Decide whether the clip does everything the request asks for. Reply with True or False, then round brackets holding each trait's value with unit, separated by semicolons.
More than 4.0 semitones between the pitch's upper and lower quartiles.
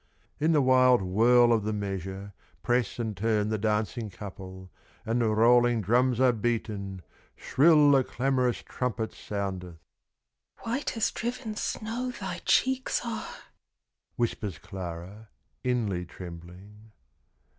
True (4.5 semitones)